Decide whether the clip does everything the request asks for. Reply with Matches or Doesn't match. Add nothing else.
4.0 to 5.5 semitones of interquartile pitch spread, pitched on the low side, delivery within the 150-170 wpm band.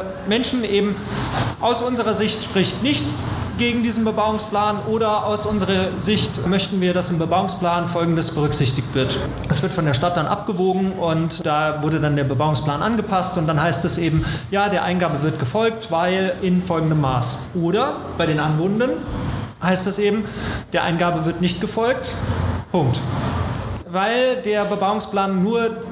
Doesn't match